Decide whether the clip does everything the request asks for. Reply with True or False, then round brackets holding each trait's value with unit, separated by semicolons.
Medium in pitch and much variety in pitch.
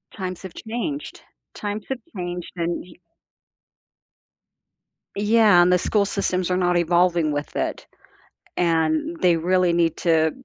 False (180 Hz; 2.7 semitones)